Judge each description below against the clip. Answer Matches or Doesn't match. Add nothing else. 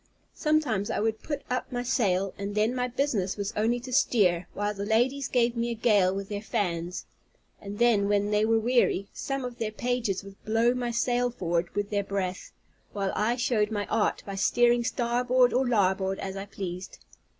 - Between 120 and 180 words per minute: Doesn't match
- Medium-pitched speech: Doesn't match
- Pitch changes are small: Doesn't match